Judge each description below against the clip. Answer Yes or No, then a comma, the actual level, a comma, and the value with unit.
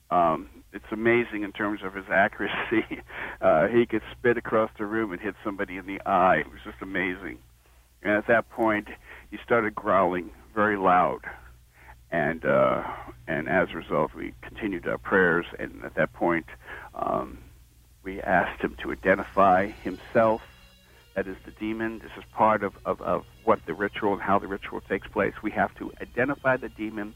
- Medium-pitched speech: No, low, 105 Hz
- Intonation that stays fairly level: No, average, 3.8 semitones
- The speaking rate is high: No, average, 175 wpm